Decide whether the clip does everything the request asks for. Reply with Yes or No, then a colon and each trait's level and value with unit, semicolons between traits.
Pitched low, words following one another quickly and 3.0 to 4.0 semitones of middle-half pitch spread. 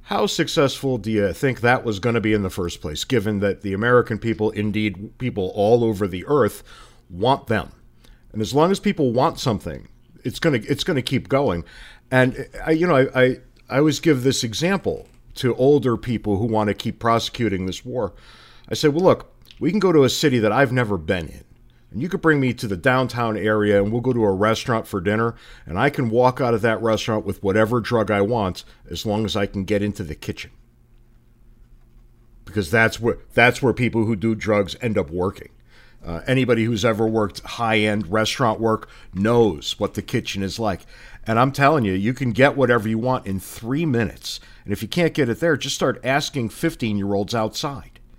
Yes: low, 115 Hz; fast, 215 wpm; average, 3.4 semitones